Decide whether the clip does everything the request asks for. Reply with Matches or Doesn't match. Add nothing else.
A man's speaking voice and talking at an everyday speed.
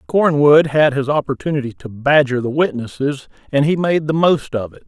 Matches